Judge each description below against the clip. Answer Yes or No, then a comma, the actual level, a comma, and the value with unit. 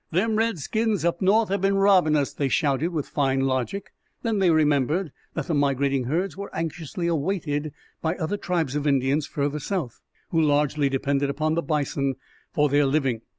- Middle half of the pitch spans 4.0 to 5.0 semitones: Yes, average, 4.3 semitones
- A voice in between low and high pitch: Yes, medium, 155 Hz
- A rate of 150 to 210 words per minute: Yes, average, 175 wpm